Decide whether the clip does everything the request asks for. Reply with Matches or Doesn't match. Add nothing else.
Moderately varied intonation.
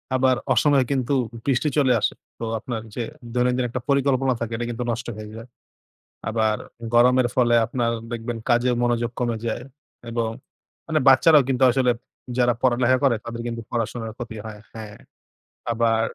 Doesn't match